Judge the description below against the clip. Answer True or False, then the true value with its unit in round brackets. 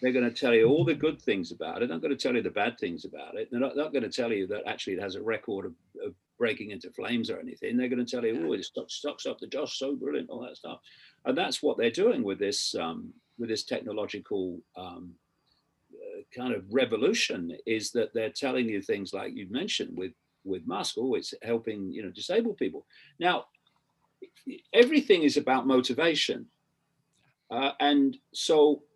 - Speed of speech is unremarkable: False (210 wpm)